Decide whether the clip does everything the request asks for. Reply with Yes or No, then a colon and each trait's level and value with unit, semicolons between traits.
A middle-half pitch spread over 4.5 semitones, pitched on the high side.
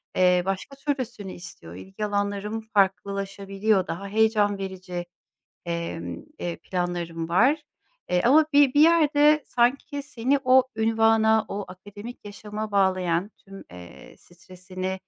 No: average, 3.8 semitones; high, 200 Hz